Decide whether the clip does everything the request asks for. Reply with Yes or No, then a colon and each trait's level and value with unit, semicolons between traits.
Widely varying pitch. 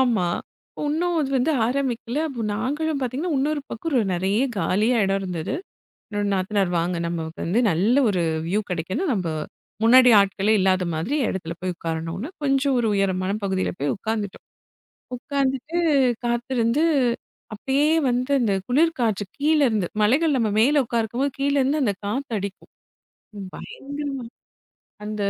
Yes: wide, 6.2 semitones